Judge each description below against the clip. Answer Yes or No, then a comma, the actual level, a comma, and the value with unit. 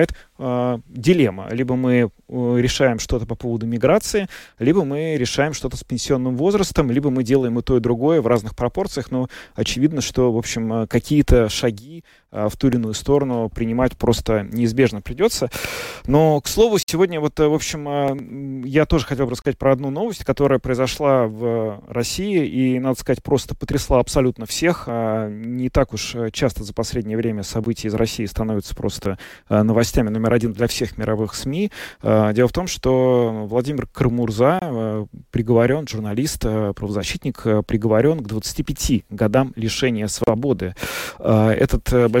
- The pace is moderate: Yes, average, 145 wpm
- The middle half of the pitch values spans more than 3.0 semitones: Yes, average, 3.5 semitones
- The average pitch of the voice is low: Yes, low, 125 Hz